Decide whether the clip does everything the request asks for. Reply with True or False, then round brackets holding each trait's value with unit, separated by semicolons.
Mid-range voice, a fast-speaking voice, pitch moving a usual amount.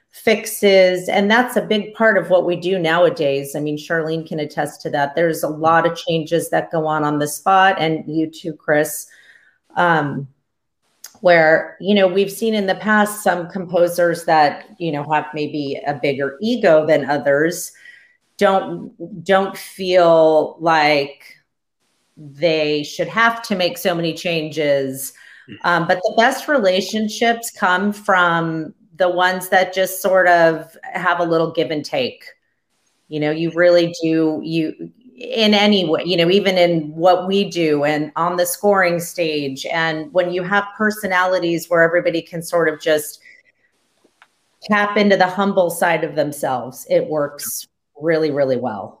False (170 Hz; 160 wpm; 3.6 semitones)